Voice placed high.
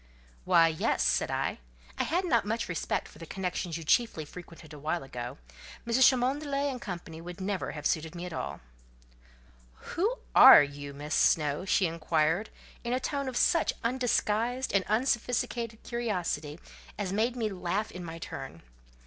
Yes: high, 195 Hz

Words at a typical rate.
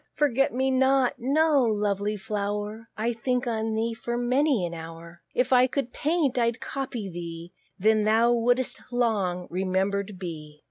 Yes: average, 150 wpm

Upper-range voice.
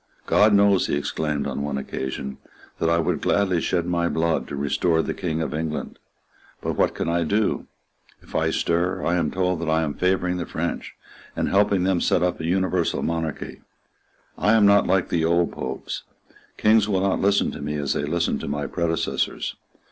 No: very low, 85 Hz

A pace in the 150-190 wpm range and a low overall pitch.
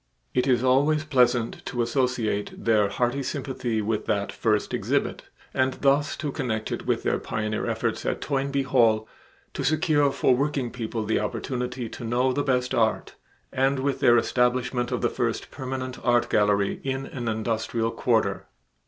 Yes: average, 160 wpm; low, 125 Hz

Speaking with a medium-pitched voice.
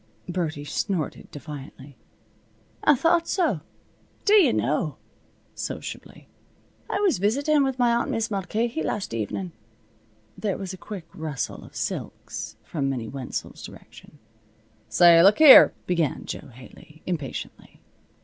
Yes: medium, 180 Hz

